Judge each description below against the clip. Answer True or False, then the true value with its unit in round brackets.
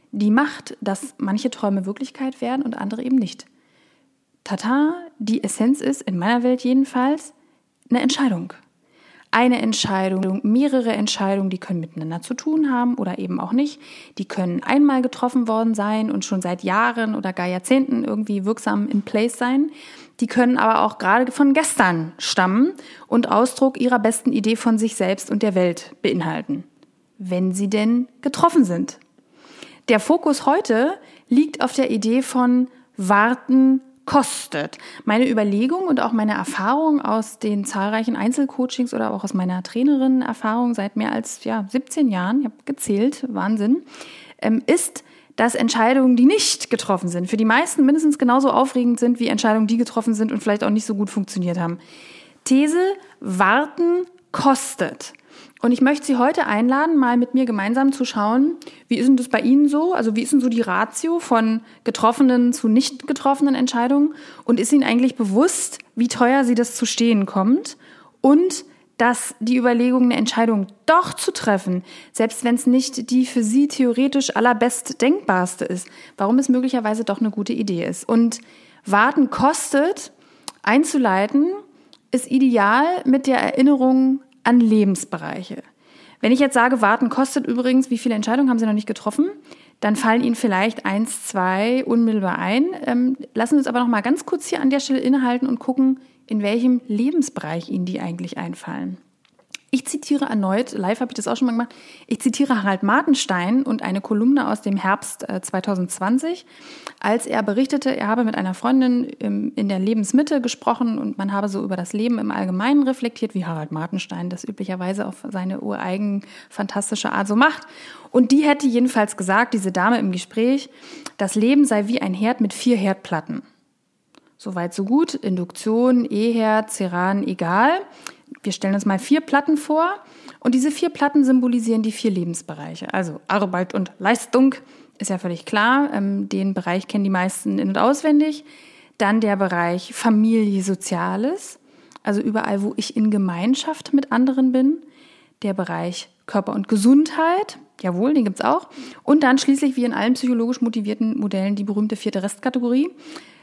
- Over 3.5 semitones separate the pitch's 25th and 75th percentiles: True (4.6 semitones)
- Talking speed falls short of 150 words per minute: False (165 wpm)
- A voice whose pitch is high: True (245 Hz)